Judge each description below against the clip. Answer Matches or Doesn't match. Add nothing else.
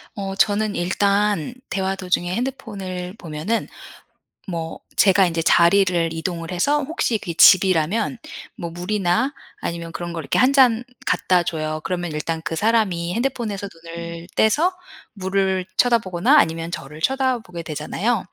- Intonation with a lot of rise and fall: Doesn't match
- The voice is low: Doesn't match